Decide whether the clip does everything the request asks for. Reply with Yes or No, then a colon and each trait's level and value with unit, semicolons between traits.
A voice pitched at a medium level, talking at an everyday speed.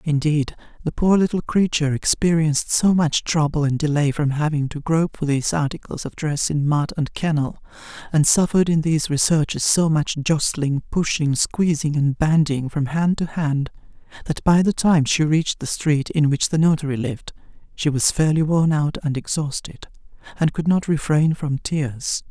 Yes: medium, 155 Hz; average, 180 wpm